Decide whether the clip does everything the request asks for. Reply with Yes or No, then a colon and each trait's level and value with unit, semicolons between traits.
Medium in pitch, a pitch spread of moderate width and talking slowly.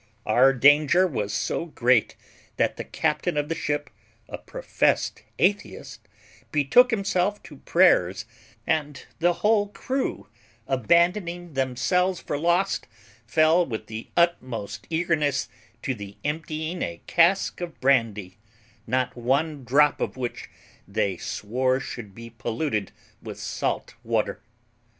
No: medium, 145 Hz; wide, 6.1 semitones; slow, 120 wpm